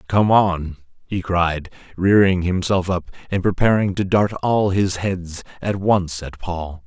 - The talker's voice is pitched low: Yes, very low, 90 Hz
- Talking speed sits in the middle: Yes, average, 155 wpm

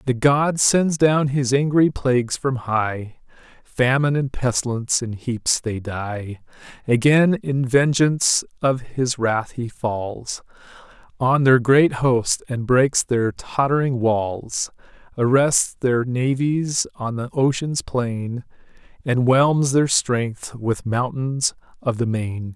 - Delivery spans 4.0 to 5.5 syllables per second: No, 3.4 syllables/s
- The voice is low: Yes, low, 125 Hz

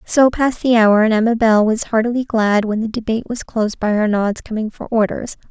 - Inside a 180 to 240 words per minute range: Yes, fast, 205 wpm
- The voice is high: Yes, high, 220 Hz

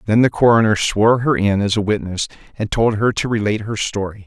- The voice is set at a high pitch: No, low, 105 Hz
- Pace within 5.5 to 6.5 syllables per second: Yes, 6.0 syllables/s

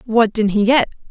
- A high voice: Yes, high, 225 Hz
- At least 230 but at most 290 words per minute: No, fast, 215 wpm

